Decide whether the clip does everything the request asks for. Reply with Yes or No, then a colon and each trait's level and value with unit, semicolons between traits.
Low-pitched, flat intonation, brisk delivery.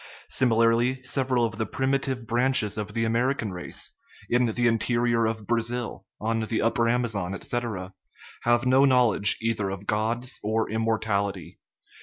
No: low, 115 Hz; narrow, 2.0 semitones; average, 150 wpm